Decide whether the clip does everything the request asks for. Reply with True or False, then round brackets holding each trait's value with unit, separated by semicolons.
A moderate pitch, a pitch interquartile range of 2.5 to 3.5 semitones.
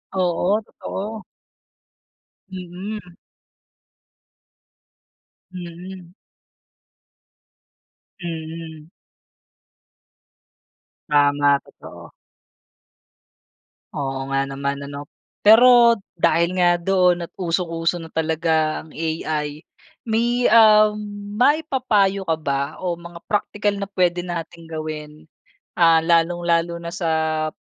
True (170 Hz; 3.2 semitones)